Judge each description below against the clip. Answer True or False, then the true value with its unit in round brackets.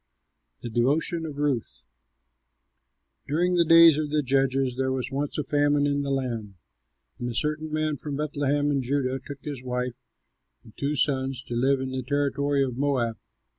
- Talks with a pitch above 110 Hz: True (140 Hz)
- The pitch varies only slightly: True (2.2 semitones)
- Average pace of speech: True (170 wpm)